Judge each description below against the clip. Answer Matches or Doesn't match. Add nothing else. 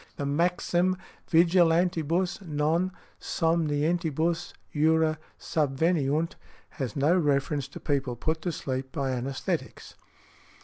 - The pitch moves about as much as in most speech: Matches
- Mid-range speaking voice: Matches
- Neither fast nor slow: Doesn't match